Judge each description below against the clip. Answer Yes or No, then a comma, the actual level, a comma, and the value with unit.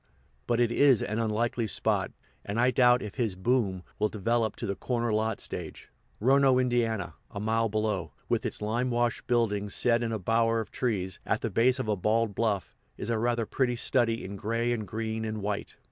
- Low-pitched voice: Yes, low, 115 Hz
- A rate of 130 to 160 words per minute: No, average, 195 wpm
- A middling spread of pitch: No, narrow, 2.1 semitones